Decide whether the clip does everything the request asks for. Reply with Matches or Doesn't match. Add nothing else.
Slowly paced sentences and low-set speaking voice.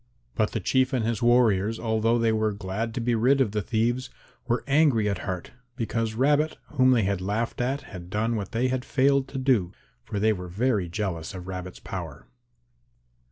Doesn't match